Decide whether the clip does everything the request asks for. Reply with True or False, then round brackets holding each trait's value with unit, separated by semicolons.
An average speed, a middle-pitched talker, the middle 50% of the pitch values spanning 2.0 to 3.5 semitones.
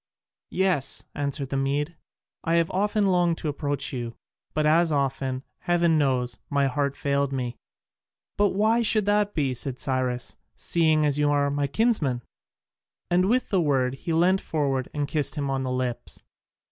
False (160 wpm; 145 Hz; 4.3 semitones)